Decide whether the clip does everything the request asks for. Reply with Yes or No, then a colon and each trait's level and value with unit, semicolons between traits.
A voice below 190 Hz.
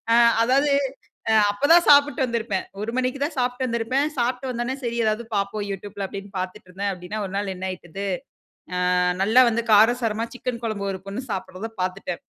No: high, 220 Hz